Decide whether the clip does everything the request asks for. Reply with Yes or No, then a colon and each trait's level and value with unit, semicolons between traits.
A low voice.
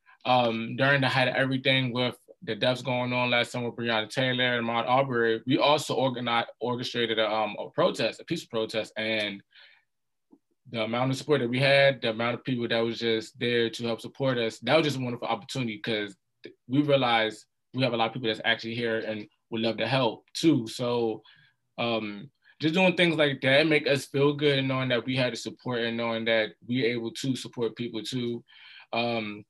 Yes: low, 120 Hz